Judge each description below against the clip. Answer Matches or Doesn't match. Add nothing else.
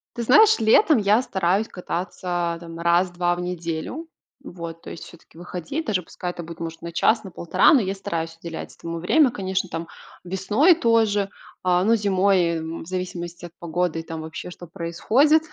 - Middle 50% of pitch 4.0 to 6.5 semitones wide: Doesn't match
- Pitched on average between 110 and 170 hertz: Doesn't match